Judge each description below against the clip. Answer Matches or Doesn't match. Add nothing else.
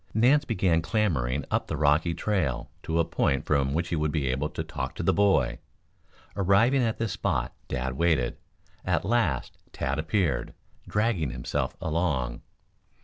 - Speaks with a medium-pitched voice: Doesn't match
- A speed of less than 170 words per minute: Matches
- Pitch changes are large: Matches